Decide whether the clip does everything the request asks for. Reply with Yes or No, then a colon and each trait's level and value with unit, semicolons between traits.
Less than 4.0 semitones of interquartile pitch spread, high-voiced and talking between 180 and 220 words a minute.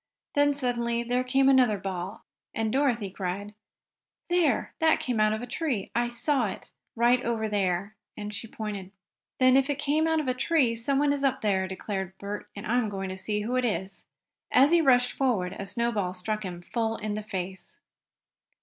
No: average, 4.3 semitones; high, 230 Hz; average, 195 wpm